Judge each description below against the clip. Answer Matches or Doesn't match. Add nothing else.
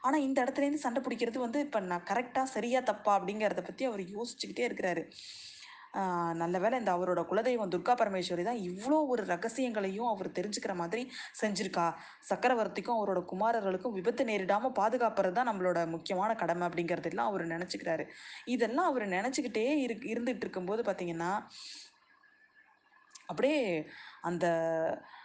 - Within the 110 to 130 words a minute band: Matches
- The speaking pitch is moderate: Doesn't match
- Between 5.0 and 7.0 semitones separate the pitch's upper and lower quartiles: Matches